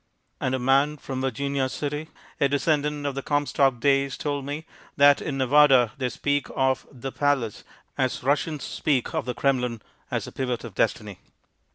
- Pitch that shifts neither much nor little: No, narrow, 1.8 semitones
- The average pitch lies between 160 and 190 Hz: No, medium, 140 Hz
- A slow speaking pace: No, average, 170 wpm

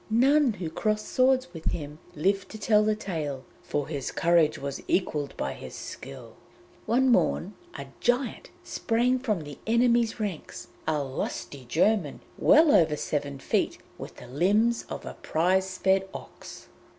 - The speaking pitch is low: No, high, 190 Hz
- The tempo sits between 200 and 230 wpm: No, average, 150 wpm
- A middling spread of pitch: No, wide, 7.4 semitones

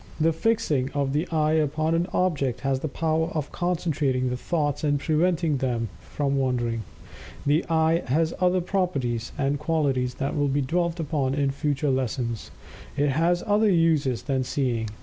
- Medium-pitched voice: Yes, medium, 145 Hz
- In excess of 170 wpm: No, average, 165 wpm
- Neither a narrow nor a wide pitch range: Yes, average, 3.7 semitones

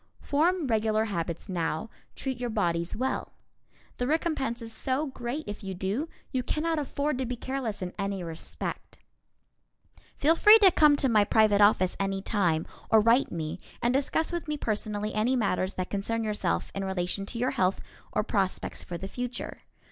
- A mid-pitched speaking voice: No, high, 220 Hz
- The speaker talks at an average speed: Yes, average, 175 wpm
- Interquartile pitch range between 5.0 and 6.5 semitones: Yes, wide, 5.4 semitones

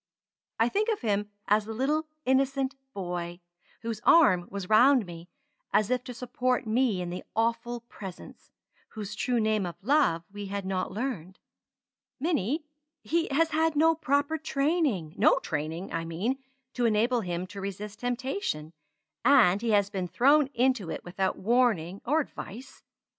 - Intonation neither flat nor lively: No, wide, 6.0 semitones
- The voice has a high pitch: Yes, high, 225 Hz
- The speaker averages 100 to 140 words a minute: No, average, 155 wpm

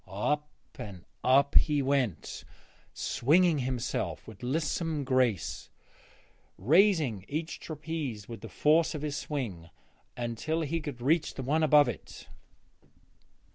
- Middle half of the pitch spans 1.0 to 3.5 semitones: No, average, 4.6 semitones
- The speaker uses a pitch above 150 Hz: No, medium, 140 Hz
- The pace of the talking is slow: Yes, slow, 120 wpm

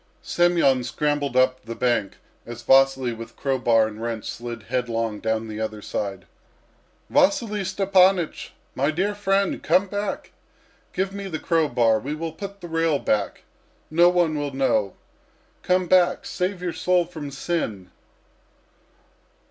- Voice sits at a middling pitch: Yes, medium, 145 Hz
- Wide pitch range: Yes, wide, 7.4 semitones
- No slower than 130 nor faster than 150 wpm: Yes, average, 145 wpm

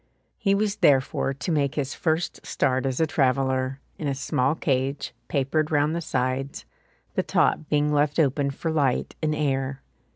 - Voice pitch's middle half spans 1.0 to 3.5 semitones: Yes, narrow, 2.4 semitones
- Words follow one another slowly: No, average, 165 wpm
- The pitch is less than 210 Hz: Yes, medium, 140 Hz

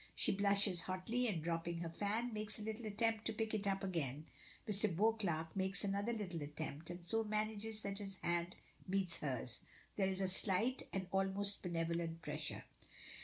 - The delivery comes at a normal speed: Yes, average, 170 wpm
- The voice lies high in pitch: Yes, high, 195 Hz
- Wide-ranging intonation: No, average, 3.8 semitones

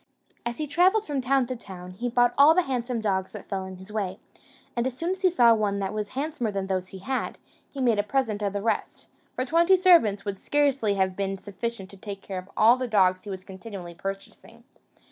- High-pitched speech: Yes, high, 215 Hz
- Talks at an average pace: No, fast, 230 wpm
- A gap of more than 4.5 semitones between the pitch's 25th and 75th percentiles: Yes, average, 5.2 semitones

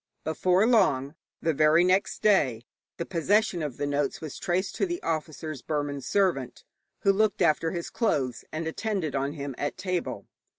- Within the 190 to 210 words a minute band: No, average, 165 wpm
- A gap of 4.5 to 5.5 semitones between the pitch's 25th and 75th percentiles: Yes, average, 4.9 semitones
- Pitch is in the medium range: Yes, medium, 160 Hz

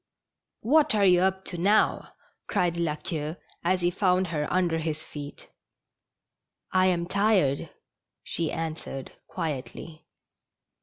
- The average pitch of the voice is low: No, medium, 175 Hz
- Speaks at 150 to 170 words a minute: No, slow, 135 wpm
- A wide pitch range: No, average, 3.0 semitones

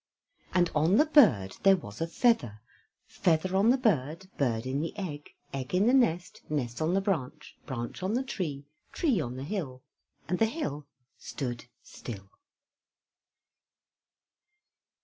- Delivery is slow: No, average, 150 wpm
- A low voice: No, medium, 160 Hz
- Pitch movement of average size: No, wide, 7.1 semitones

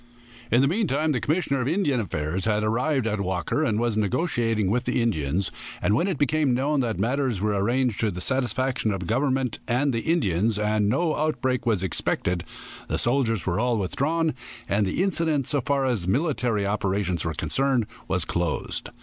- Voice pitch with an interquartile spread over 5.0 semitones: Yes, wide, 5.4 semitones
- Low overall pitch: Yes, low, 120 Hz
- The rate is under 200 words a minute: Yes, average, 185 wpm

